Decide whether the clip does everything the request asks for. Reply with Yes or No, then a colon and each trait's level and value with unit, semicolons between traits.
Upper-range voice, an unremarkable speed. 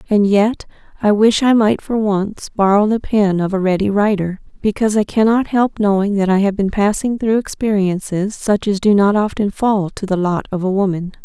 No: high, 205 Hz; fast, 210 wpm